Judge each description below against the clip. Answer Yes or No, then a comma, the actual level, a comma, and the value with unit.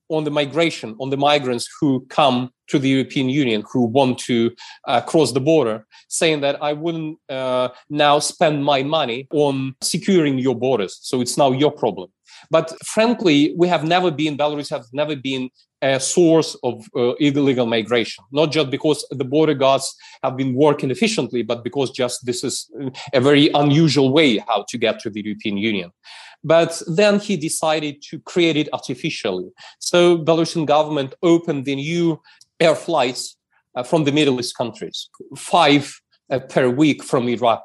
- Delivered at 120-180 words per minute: Yes, average, 170 wpm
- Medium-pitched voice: Yes, medium, 145 Hz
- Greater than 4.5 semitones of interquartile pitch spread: No, average, 3.8 semitones